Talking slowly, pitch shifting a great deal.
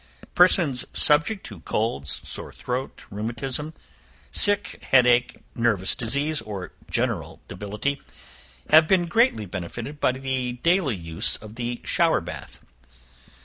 Yes: slow, 120 wpm; wide, 6.3 semitones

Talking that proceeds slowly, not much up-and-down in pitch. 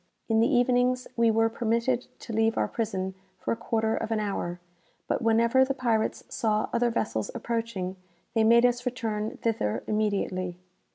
No: average, 165 wpm; narrow, 1.9 semitones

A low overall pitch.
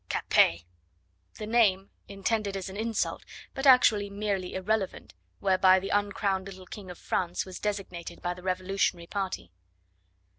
No: high, 195 Hz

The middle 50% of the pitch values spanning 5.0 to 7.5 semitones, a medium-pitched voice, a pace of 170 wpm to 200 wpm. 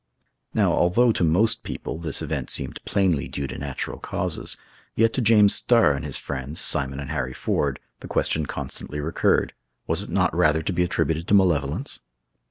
No: wide, 5.4 semitones; very low, 80 Hz; average, 180 wpm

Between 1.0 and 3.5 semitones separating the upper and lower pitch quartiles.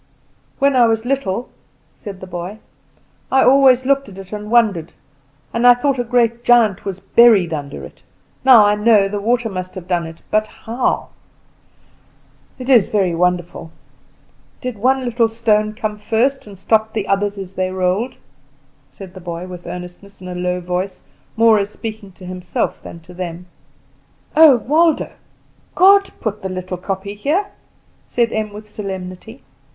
No: average, 4.5 semitones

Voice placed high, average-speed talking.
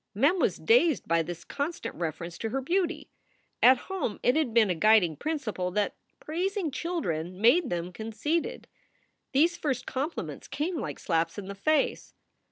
Yes: very high, 250 Hz; average, 165 wpm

